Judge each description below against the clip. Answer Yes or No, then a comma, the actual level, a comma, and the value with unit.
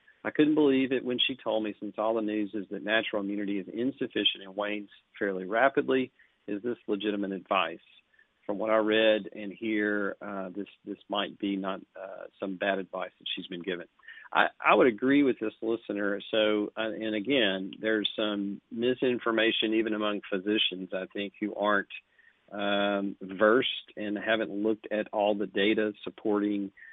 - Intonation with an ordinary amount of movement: No, narrow, 1.6 semitones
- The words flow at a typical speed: Yes, average, 170 wpm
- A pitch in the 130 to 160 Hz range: No, low, 105 Hz